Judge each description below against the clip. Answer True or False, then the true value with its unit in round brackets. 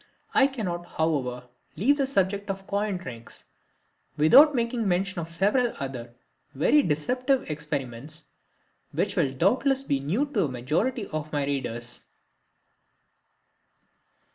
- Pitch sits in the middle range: True (175 Hz)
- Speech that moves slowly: True (120 wpm)